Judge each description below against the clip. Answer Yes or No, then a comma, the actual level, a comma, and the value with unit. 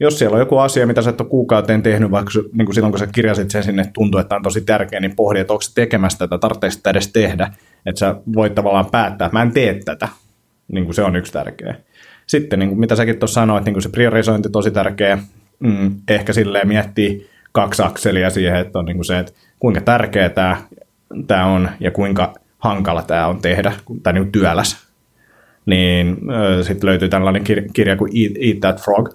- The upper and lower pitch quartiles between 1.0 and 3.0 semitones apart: Yes, narrow, 2.5 semitones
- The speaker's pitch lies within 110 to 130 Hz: No, low, 100 Hz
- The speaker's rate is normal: No, fast, 200 wpm